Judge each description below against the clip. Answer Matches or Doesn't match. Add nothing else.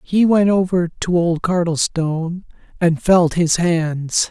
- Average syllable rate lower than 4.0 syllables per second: Matches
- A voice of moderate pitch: Matches